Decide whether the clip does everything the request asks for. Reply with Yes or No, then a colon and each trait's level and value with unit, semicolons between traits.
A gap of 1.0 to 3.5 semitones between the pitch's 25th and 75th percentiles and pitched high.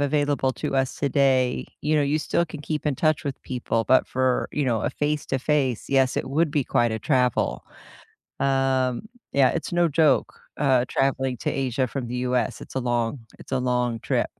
No: narrow, 2.6 semitones; low, 135 Hz